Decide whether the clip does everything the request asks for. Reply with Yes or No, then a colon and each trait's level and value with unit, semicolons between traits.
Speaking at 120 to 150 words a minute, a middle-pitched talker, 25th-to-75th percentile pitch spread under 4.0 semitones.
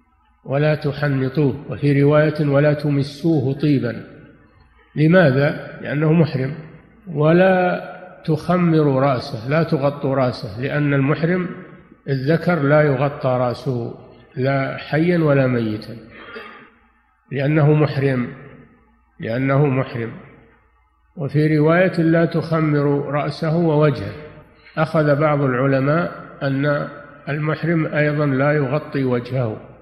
No: average, 90 wpm; medium, 145 Hz; average, 2.7 semitones